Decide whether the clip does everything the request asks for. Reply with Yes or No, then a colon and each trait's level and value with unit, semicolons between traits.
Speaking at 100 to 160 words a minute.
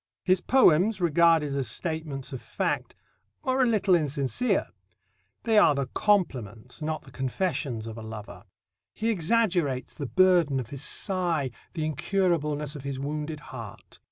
Yes: average, 145 wpm